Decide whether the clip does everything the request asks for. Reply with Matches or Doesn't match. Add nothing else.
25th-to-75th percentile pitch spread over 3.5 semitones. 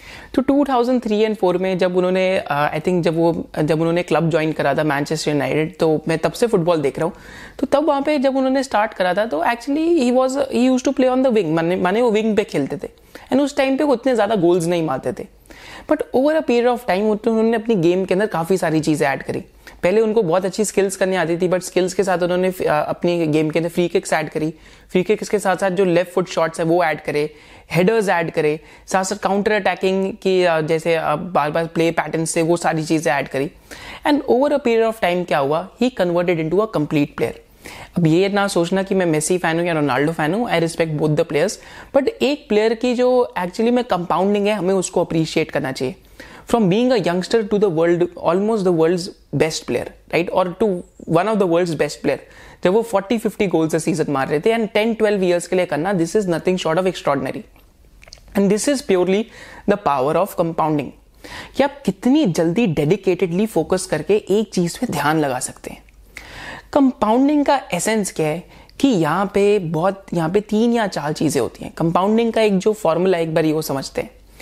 Matches